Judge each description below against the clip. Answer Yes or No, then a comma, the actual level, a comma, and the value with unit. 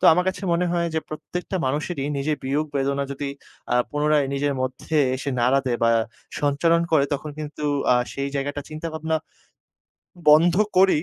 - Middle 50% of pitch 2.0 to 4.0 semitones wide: Yes, narrow, 2.4 semitones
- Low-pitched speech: No, medium, 150 Hz